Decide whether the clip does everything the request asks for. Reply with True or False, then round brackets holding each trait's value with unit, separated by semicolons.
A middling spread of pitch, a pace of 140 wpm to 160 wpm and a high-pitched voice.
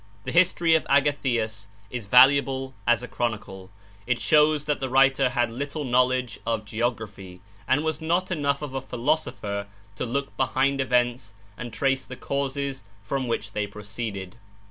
False (3.8 semitones; 155 wpm; 130 Hz)